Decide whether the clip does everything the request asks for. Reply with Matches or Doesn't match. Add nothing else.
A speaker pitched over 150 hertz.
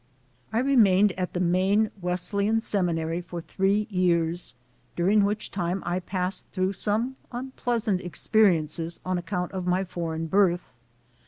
Matches